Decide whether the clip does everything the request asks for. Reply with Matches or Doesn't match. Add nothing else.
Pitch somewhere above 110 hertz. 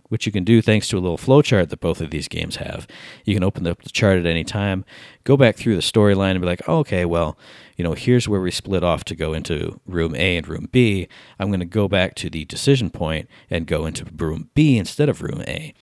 Doesn't match